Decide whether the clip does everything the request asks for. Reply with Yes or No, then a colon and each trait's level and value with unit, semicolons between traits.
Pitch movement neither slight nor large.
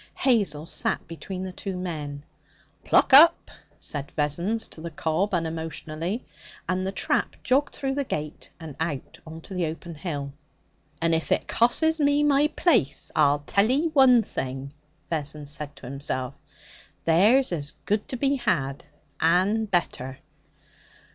No: wide, 7.4 semitones